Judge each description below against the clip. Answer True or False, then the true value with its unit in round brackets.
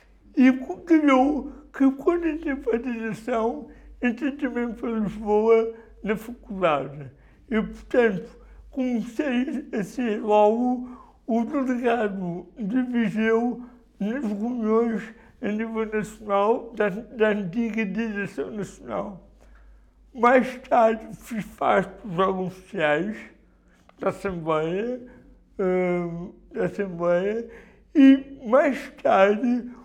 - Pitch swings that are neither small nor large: True (3.6 semitones)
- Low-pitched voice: False (225 Hz)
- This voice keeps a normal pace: False (95 wpm)